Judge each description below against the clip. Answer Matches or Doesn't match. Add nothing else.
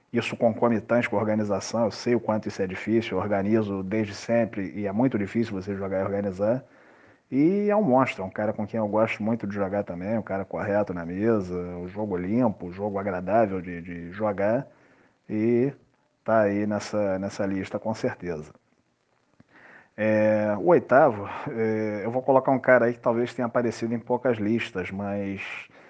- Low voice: Matches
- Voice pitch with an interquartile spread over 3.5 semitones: Doesn't match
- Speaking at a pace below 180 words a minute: Doesn't match